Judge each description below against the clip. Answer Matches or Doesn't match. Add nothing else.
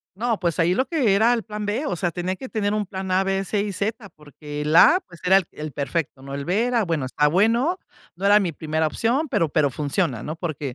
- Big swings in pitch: Matches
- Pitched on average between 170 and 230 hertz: Matches